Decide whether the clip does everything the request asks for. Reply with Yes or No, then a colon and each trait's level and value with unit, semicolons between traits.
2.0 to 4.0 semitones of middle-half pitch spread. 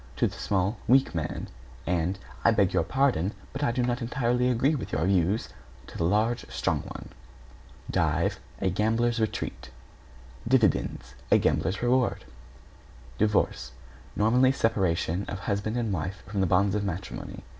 No: average, 4.5 semitones